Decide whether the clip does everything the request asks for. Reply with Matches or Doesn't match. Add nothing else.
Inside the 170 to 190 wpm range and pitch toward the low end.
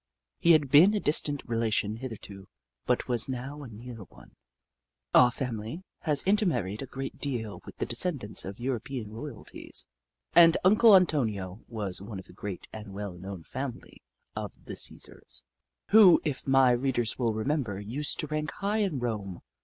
Doesn't match